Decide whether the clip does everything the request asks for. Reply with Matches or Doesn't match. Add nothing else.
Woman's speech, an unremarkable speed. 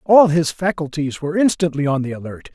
Doesn't match